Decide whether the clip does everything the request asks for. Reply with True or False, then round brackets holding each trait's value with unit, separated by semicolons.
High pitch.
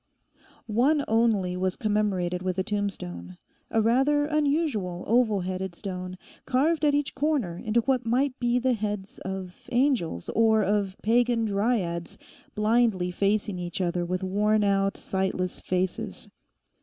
True (210 Hz)